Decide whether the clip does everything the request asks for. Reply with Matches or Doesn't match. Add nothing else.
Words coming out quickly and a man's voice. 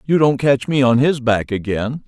Matches